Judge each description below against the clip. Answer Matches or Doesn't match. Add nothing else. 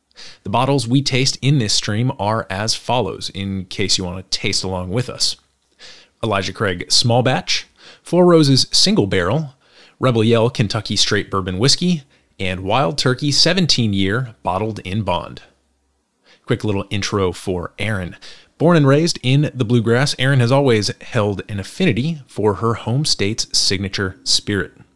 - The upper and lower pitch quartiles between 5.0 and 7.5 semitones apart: Matches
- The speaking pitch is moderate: Doesn't match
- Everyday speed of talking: Matches